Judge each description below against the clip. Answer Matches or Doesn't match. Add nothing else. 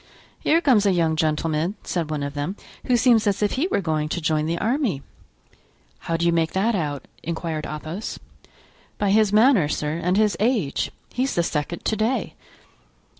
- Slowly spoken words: Doesn't match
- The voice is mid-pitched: Matches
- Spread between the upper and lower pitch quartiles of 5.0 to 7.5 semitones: Matches